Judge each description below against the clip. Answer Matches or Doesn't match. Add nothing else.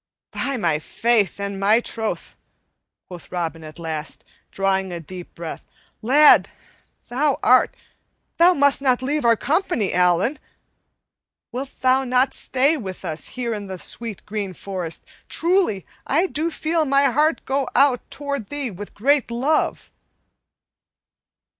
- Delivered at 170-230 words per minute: Doesn't match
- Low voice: Doesn't match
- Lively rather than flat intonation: Matches